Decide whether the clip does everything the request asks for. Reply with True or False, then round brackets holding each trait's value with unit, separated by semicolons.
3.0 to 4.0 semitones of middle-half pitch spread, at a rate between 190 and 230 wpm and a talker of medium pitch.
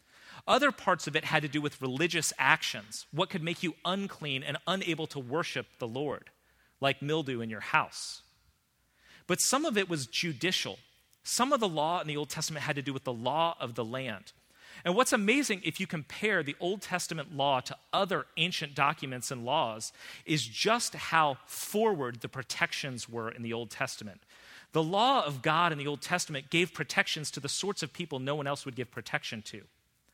False (4.5 semitones; 195 wpm; 155 Hz)